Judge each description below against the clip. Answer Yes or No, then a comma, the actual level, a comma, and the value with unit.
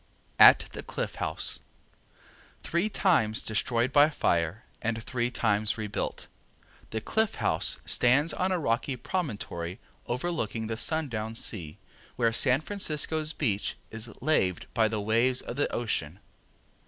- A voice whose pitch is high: No, low, 120 Hz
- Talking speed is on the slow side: Yes, slow, 130 wpm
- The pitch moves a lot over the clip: Yes, wide, 5.7 semitones